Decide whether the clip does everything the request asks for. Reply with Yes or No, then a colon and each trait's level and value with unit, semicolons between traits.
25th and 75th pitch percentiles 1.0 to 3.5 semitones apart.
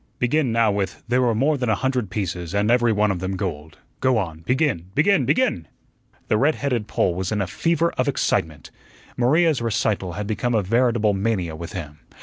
No: average, 5.3 semitones